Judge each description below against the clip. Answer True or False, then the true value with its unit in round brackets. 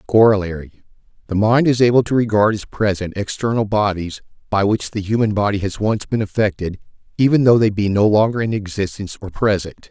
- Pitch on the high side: False (105 Hz)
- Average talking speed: True (175 wpm)